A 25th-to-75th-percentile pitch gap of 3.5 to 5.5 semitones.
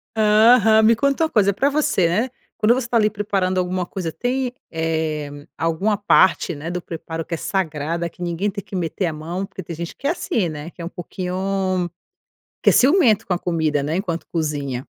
Yes: average, 4.6 semitones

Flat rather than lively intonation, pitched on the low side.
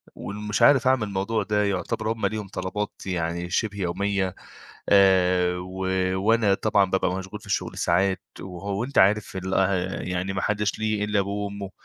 Yes: narrow, 2.0 semitones; low, 100 Hz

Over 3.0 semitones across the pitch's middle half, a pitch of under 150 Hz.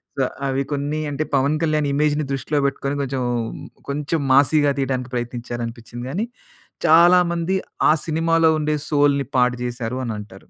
Yes: average, 3.5 semitones; medium, 140 Hz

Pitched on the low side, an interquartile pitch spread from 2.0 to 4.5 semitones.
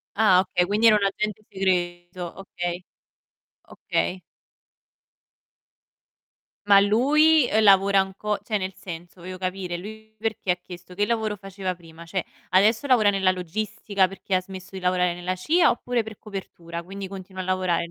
No: high, 190 Hz; average, 2.7 semitones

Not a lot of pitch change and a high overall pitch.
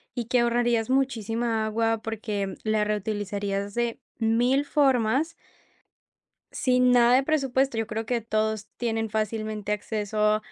Yes: narrow, 2.3 semitones; high, 225 Hz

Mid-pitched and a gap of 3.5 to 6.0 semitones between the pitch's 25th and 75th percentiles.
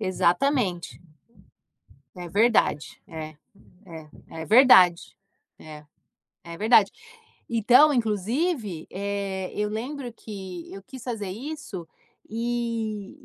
No: high, 205 Hz; average, 5.0 semitones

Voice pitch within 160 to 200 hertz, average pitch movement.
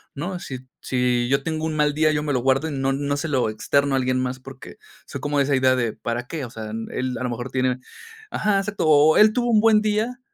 No: medium, 140 Hz; average, 3.7 semitones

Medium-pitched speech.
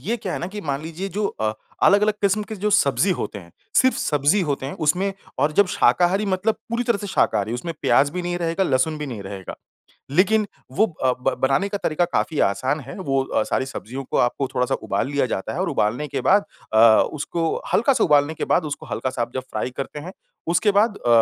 Yes: medium, 160 Hz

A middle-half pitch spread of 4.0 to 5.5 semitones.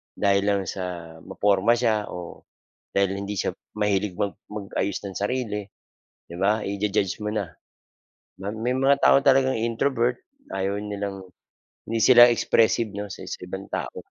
No: average, 2.7 semitones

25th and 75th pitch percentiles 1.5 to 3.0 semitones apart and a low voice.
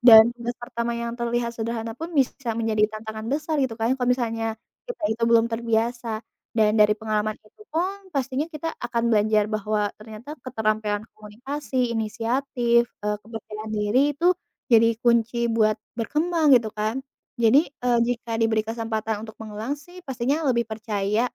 No: narrow, 2.6 semitones; high, 230 Hz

